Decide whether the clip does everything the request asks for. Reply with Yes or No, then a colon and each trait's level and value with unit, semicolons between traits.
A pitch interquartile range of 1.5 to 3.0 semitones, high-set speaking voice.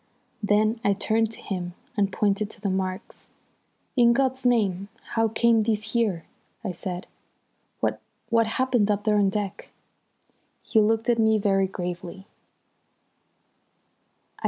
Yes: narrow, 2.6 semitones; high, 210 Hz